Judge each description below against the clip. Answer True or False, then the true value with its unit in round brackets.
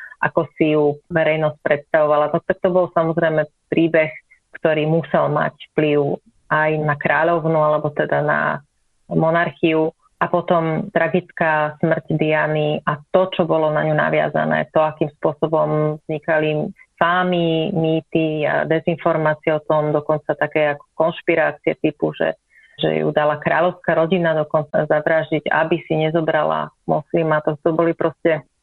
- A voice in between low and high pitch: True (155 Hz)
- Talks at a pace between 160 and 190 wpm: False (140 wpm)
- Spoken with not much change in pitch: True (1.6 semitones)